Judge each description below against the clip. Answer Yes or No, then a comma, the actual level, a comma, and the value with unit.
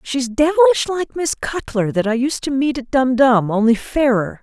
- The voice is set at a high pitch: Yes, very high, 260 Hz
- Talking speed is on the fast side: No, average, 190 wpm